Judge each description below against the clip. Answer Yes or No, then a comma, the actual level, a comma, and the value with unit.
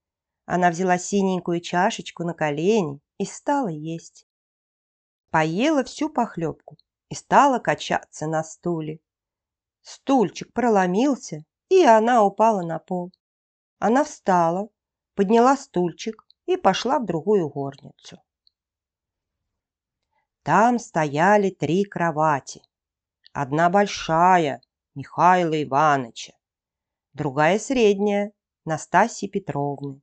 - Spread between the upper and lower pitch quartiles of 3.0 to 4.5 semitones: No, wide, 5.6 semitones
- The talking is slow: Yes, slow, 90 wpm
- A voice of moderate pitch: Yes, medium, 175 Hz